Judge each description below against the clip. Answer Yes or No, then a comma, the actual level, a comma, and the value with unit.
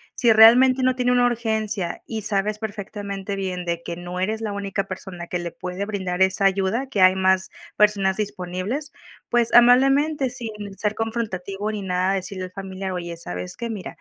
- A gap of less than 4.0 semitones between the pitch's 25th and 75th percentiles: Yes, average, 3.2 semitones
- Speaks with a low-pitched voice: No, high, 200 Hz